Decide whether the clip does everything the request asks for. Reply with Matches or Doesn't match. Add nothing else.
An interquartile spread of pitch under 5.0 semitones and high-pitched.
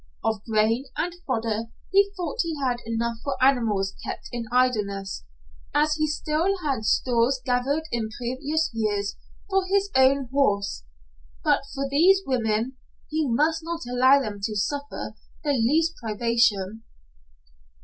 Doesn't match